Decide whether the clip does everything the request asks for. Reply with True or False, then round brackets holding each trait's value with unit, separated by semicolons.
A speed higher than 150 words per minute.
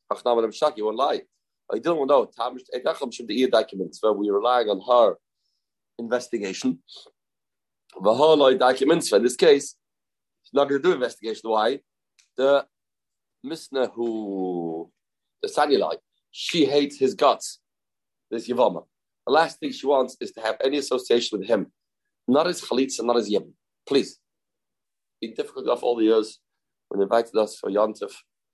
False (135 wpm)